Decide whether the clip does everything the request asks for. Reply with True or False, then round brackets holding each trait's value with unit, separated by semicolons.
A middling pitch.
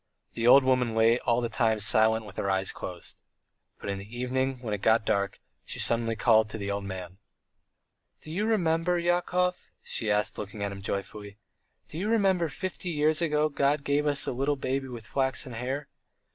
False (125 Hz)